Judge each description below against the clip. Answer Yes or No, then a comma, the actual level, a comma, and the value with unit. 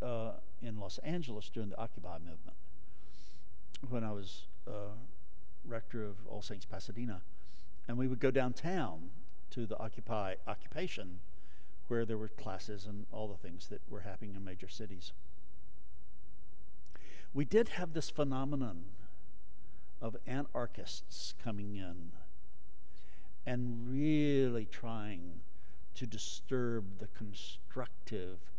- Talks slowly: Yes, slow, 120 wpm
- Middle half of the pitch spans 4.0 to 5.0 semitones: Yes, average, 4.6 semitones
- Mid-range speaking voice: No, low, 100 Hz